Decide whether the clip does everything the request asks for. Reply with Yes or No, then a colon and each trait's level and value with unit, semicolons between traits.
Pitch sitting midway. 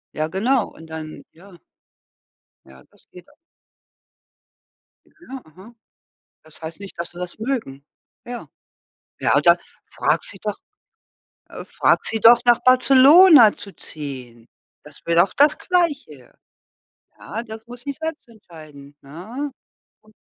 No: high, 210 Hz